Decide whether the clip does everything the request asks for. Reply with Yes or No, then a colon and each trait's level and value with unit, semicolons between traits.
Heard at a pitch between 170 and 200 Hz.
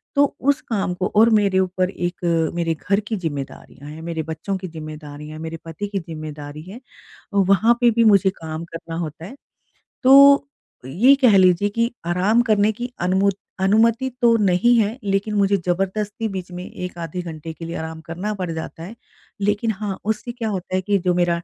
Yes: high, 190 Hz